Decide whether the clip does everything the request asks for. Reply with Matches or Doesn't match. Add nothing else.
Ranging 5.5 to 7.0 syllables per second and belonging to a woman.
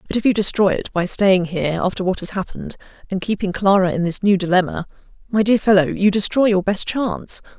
Matches